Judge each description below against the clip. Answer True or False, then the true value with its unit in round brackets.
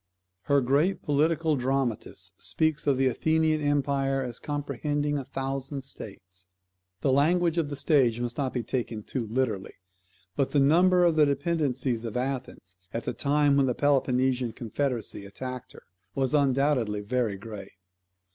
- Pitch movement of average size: True (3.1 semitones)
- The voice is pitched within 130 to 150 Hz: True (135 Hz)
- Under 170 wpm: True (150 wpm)